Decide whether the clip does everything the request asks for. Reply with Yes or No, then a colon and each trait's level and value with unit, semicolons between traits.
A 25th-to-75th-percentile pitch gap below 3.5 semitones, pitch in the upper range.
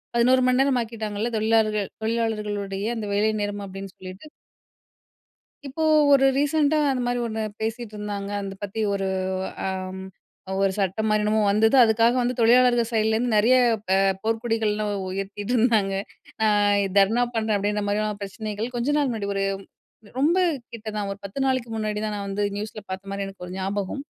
Yes: average, 2.7 semitones; high, 215 Hz